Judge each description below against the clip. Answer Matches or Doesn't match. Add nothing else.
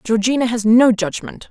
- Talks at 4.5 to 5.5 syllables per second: Matches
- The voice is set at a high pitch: Matches